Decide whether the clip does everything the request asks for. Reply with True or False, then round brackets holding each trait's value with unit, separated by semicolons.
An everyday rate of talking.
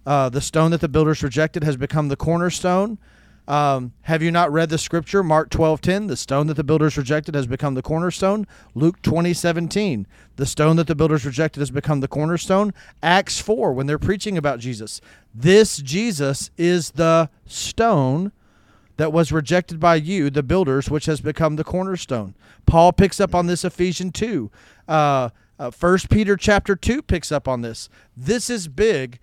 True (180 wpm)